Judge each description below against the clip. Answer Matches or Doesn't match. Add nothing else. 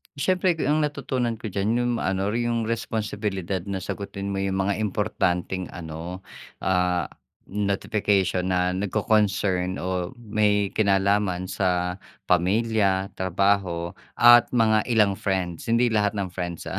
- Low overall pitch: Matches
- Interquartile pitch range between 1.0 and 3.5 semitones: Matches